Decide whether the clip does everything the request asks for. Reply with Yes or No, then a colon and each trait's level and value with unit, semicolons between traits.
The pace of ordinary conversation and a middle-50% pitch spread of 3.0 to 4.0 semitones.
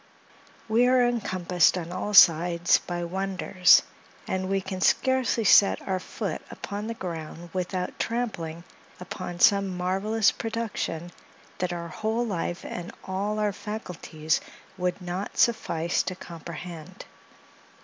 No: slow, 125 wpm; average, 3.3 semitones